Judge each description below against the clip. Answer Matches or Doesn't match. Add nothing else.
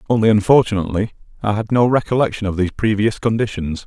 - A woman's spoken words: Doesn't match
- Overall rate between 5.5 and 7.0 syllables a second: Matches